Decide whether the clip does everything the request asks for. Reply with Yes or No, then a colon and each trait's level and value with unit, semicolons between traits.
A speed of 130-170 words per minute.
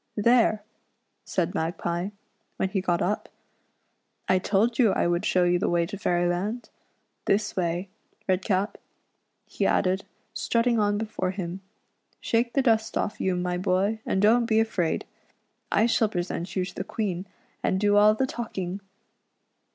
Yes: average, 160 wpm